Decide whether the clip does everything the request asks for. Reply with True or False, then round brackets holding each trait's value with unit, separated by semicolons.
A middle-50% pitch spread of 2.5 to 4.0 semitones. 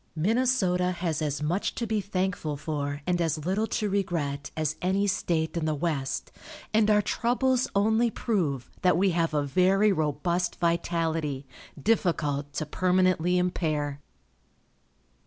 False (4.4 semitones)